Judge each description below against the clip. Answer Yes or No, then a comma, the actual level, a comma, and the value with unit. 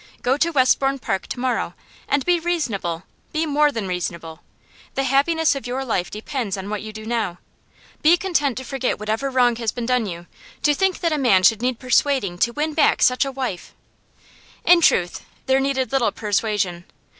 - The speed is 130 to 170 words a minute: No, average, 190 wpm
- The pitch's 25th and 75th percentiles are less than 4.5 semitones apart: No, average, 5.1 semitones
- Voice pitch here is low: No, very high, 250 Hz